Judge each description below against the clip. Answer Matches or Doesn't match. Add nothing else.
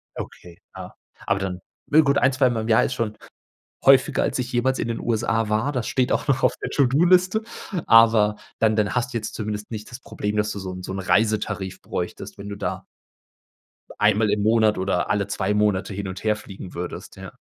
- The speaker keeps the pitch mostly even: Doesn't match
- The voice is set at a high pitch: Doesn't match